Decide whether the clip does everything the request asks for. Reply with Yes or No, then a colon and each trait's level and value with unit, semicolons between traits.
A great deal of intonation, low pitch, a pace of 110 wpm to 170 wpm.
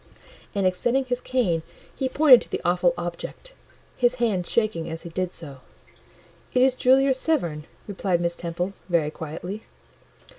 No: wide, 6.7 semitones; medium, 185 Hz; average, 150 wpm